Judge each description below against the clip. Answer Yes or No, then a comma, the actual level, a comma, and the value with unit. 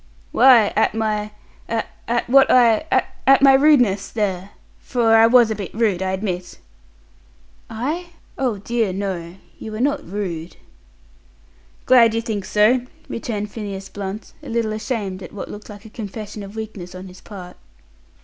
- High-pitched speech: Yes, high, 215 Hz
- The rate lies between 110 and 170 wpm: Yes, average, 155 wpm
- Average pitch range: Yes, average, 3.0 semitones